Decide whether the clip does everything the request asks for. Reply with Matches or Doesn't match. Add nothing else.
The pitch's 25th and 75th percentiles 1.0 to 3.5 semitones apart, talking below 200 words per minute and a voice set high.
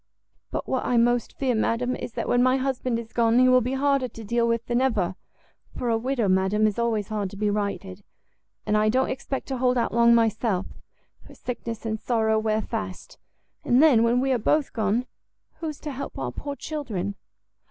Doesn't match